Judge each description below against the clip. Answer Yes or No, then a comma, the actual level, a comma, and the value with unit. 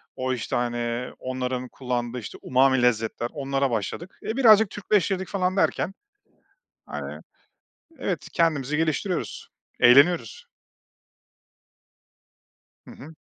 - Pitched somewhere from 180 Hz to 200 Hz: No, low, 135 Hz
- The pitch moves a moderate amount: No, wide, 6.5 semitones